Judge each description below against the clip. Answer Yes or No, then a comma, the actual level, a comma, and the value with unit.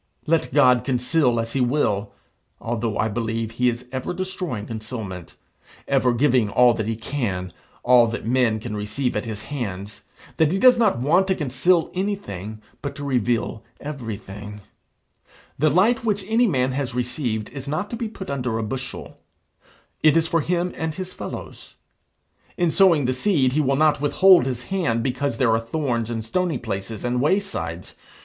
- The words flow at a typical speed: Yes, average, 170 wpm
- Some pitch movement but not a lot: No, wide, 5.9 semitones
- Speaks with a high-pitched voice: No, low, 125 Hz